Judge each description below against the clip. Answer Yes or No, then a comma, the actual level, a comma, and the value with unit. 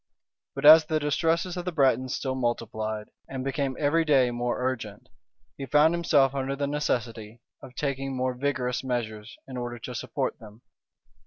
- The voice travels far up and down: No, average, 3.3 semitones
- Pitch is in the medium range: No, low, 130 Hz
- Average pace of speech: Yes, average, 165 wpm